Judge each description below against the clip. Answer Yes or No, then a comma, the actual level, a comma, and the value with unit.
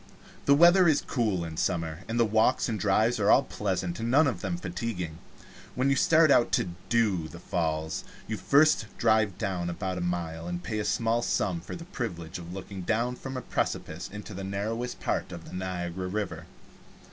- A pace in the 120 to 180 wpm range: No, average, 195 wpm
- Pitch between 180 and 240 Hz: No, low, 100 Hz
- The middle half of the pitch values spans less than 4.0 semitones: No, average, 5.2 semitones